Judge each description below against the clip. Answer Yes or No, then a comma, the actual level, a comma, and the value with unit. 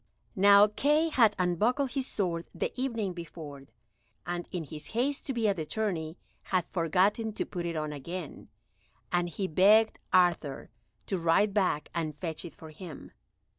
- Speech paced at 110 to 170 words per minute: Yes, average, 165 wpm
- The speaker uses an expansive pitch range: No, average, 4.6 semitones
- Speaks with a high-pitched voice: No, medium, 180 Hz